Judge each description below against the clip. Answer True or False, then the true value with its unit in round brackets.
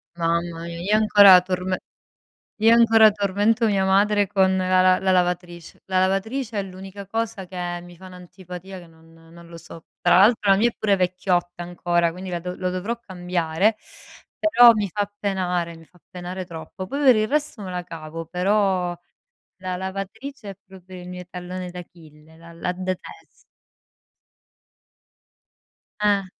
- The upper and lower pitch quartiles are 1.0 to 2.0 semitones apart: False (2.4 semitones)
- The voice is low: False (185 Hz)